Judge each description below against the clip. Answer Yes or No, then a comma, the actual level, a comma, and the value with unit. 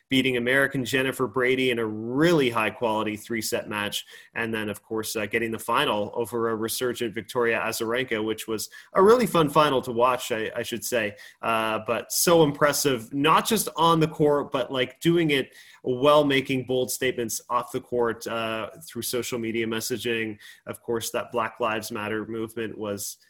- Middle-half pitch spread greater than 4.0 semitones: No, average, 2.8 semitones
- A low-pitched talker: Yes, low, 120 Hz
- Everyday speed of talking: Yes, average, 180 wpm